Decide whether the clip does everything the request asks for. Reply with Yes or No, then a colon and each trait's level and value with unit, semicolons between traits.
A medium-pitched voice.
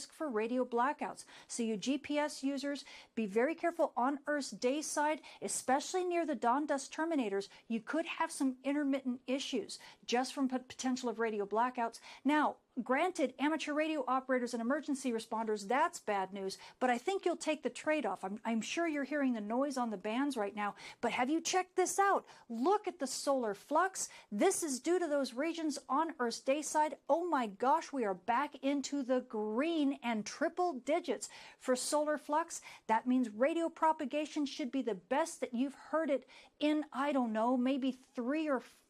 No: very high, 275 Hz